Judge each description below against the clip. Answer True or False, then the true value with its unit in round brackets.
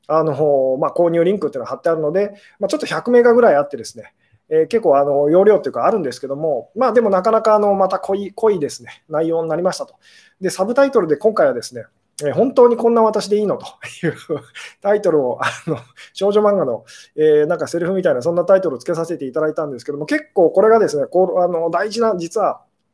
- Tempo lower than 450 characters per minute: False (470 characters per minute)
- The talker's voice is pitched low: False (190 Hz)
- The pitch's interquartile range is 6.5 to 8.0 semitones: False (5.5 semitones)